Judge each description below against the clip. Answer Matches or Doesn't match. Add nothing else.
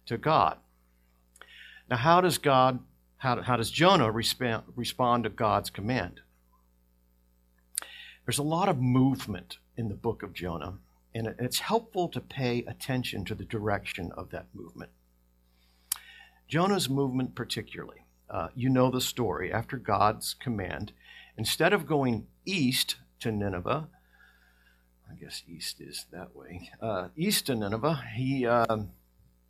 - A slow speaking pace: Matches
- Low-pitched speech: Matches